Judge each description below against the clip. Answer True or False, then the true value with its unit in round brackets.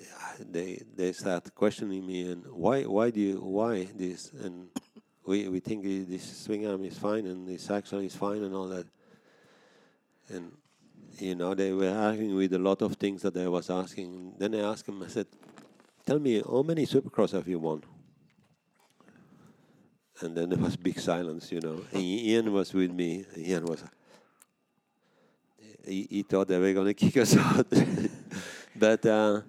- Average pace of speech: True (170 wpm)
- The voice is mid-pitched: False (95 Hz)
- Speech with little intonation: True (2.0 semitones)